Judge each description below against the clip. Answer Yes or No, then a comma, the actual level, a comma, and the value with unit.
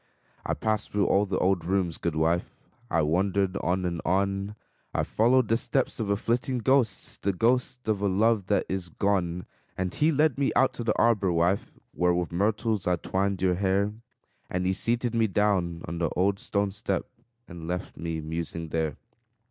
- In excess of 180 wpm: Yes, average, 190 wpm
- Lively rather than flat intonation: No, average, 3.6 semitones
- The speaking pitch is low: Yes, very low, 95 Hz